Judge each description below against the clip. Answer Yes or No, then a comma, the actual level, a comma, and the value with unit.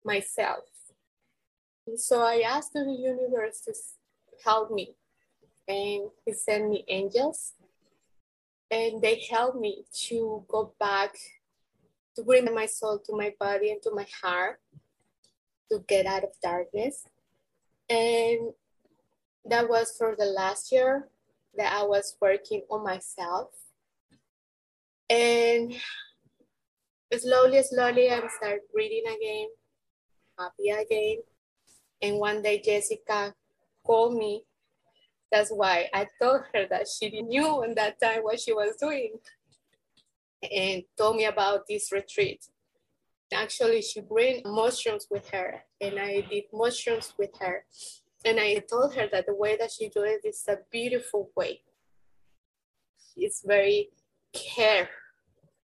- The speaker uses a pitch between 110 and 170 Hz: No, high, 225 Hz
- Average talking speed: No, slow, 125 wpm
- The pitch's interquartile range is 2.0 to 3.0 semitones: No, average, 5.2 semitones